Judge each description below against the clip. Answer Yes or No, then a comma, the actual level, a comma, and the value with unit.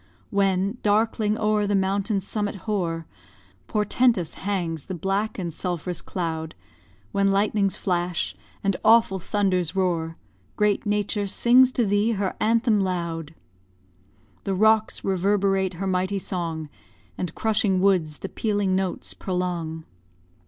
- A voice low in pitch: No, high, 195 Hz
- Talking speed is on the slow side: Yes, slow, 125 wpm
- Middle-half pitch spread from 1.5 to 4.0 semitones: Yes, narrow, 2.6 semitones